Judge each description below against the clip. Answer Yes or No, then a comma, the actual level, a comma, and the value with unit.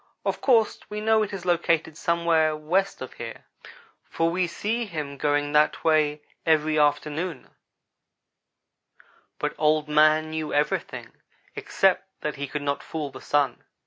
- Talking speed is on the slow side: No, average, 145 wpm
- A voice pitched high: No, medium, 155 Hz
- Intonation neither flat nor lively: No, narrow, 2.3 semitones